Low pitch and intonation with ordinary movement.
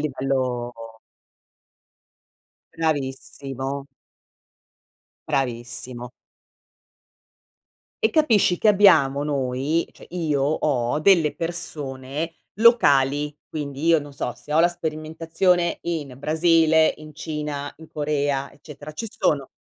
No: medium, 150 Hz; average, 3.2 semitones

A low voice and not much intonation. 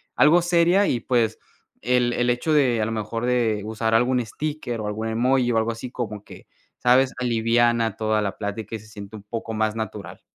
Yes: low, 115 Hz; narrow, 2.3 semitones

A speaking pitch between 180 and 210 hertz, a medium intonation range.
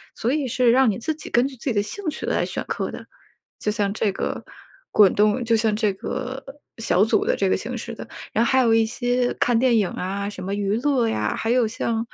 No: high, 225 Hz; average, 3.2 semitones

